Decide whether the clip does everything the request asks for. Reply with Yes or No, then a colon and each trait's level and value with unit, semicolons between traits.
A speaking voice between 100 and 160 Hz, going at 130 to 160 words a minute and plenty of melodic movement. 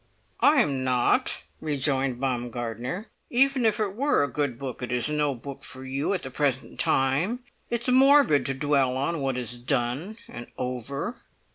No: medium, 140 Hz; average, 170 wpm; wide, 6.4 semitones